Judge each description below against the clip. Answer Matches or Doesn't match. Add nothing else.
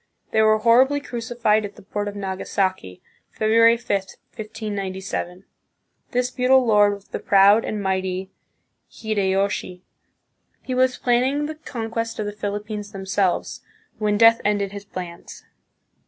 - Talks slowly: Matches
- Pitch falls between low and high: Doesn't match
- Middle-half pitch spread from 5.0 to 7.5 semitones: Doesn't match